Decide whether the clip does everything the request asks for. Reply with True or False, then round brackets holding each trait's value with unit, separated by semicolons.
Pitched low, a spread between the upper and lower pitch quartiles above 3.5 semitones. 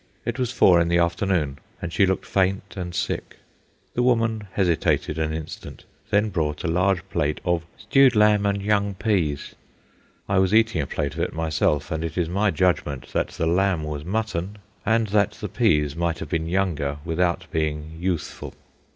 True (90 Hz; 4.0 semitones)